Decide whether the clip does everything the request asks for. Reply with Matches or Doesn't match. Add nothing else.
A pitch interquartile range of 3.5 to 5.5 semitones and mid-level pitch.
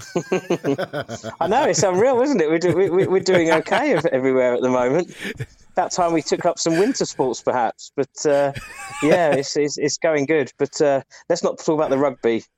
Matches